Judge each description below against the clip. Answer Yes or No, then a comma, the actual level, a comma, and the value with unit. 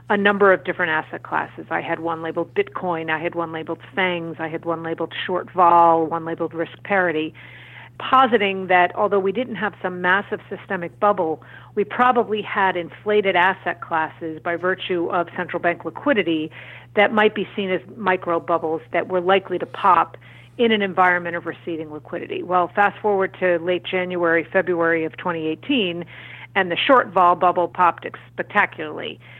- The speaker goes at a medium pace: Yes, average, 165 wpm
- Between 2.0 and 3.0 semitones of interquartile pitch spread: Yes, average, 2.7 semitones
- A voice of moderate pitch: Yes, medium, 180 Hz